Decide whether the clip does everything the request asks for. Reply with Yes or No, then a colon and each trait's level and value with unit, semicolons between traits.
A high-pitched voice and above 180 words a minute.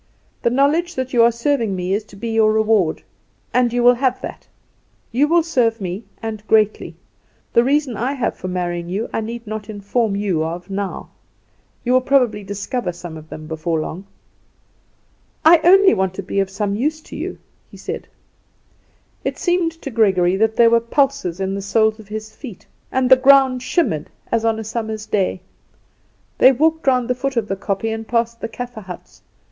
Yes: high, 225 Hz; average, 190 wpm